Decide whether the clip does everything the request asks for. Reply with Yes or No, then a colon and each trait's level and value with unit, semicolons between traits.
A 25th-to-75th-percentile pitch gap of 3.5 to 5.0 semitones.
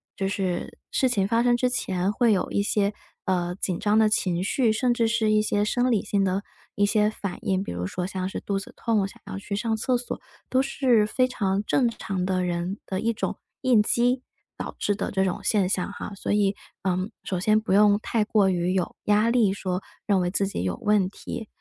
No: average, 2.8 semitones